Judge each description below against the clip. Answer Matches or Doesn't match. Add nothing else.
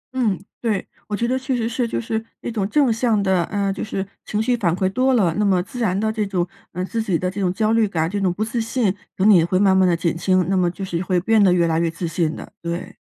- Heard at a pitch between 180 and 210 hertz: Matches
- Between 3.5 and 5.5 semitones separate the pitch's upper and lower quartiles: Matches